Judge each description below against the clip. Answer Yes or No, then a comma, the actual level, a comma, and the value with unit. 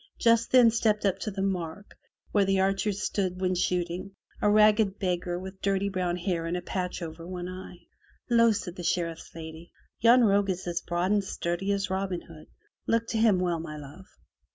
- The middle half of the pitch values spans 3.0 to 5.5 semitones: No, narrow, 2.5 semitones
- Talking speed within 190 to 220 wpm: Yes, average, 195 wpm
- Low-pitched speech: No, medium, 185 Hz